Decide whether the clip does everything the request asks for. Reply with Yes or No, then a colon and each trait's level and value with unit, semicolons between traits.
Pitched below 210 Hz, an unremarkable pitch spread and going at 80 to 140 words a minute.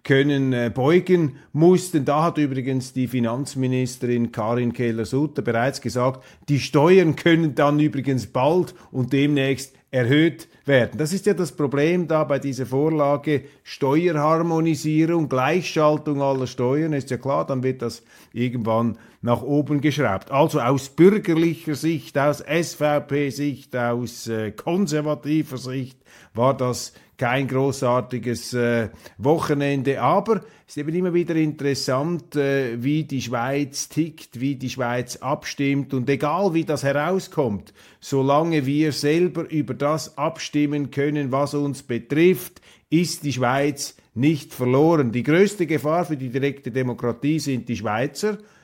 Yes: medium, 140 Hz; average, 3.3 semitones; average, 130 wpm